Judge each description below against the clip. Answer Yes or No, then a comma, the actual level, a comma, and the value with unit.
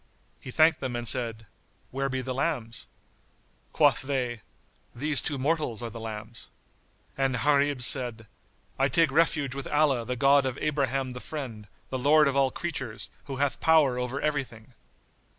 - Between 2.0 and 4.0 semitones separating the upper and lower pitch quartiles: Yes, average, 2.9 semitones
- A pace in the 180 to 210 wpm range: No, average, 160 wpm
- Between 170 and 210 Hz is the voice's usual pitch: No, low, 135 Hz